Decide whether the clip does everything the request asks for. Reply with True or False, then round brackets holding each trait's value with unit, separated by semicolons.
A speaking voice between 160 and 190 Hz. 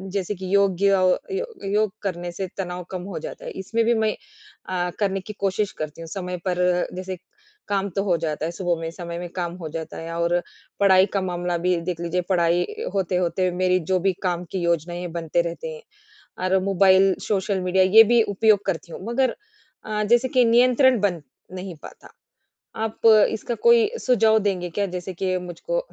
True (185 Hz)